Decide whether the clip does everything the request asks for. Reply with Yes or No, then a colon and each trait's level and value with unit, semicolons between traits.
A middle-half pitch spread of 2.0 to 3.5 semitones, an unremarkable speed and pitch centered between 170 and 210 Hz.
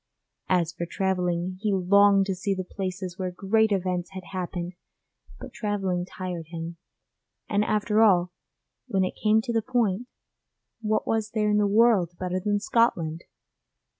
Yes: average, 2.7 semitones; average, 155 wpm; high, 190 Hz